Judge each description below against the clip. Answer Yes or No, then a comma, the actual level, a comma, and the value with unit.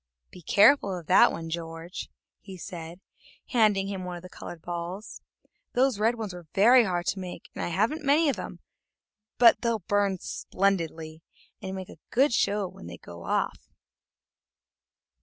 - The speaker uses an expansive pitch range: No, average, 4.1 semitones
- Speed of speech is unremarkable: Yes, average, 165 wpm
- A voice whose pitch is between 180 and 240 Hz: Yes, high, 190 Hz